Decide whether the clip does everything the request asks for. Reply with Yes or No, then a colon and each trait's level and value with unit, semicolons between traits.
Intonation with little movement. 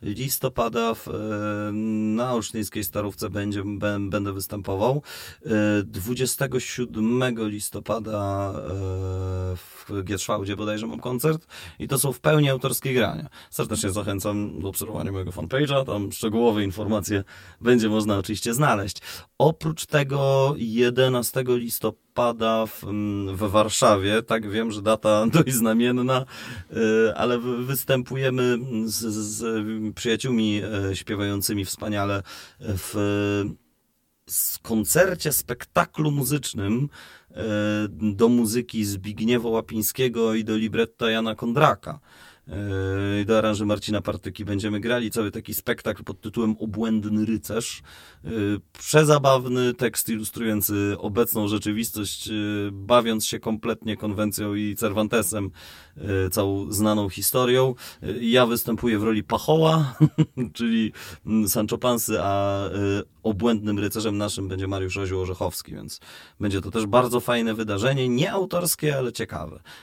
No: average, 3.0 semitones